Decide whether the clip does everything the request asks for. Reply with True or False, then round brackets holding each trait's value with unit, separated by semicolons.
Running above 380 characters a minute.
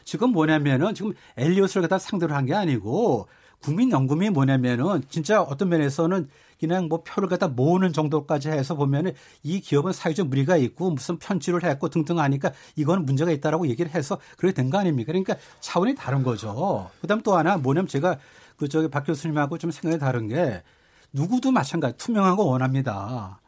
True (405 characters per minute)